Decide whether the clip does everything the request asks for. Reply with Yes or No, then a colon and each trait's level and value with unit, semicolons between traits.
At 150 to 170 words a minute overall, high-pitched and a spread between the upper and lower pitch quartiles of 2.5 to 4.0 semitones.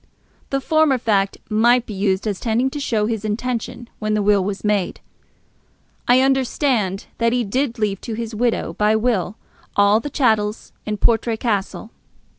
Yes: average, 165 wpm; high, 220 Hz; average, 2.9 semitones